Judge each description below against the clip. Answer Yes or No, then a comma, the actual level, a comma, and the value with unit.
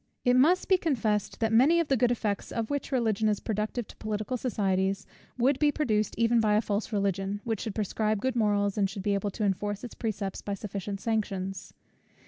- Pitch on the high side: Yes, high, 215 Hz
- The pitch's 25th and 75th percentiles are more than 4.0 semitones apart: No, average, 3.1 semitones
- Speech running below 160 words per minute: No, fast, 205 wpm